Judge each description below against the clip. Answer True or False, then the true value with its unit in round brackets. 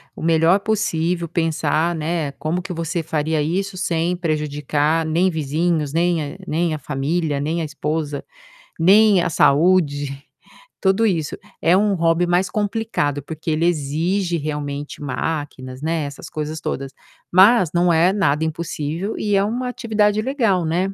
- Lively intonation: False (3.4 semitones)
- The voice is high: False (165 Hz)